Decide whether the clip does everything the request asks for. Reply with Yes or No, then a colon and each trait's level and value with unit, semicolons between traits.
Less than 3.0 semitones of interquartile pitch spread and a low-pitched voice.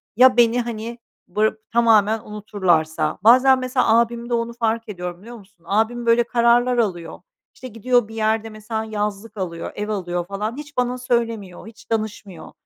No: narrow, 2.5 semitones; high, 225 Hz